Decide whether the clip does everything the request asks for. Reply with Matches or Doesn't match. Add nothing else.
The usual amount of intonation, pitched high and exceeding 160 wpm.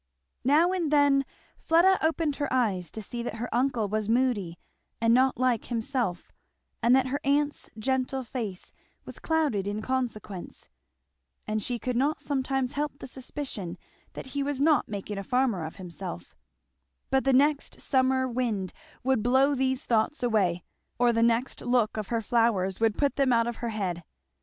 Matches